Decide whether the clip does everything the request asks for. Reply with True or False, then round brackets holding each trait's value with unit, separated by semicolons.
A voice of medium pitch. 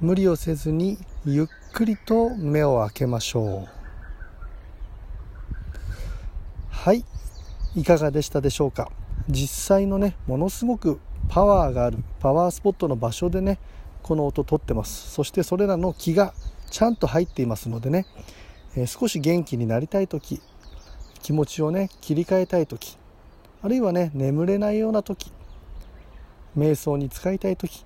True (150 Hz)